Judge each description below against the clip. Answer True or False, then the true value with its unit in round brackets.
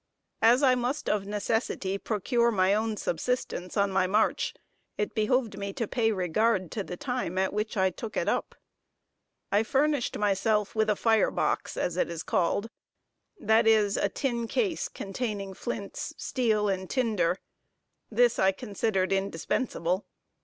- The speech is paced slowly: False (155 wpm)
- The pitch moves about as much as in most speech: True (3.4 semitones)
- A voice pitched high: True (210 Hz)